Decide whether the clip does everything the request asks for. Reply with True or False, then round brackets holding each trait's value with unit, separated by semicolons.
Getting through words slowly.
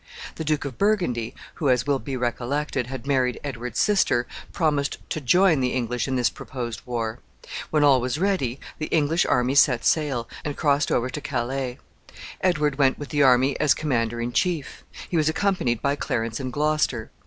False (180 wpm)